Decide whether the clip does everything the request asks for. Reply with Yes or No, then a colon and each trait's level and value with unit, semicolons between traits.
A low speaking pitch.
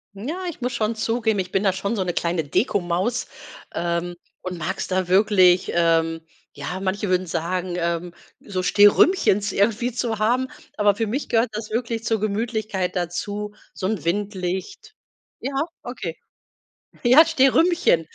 No: high, 200 Hz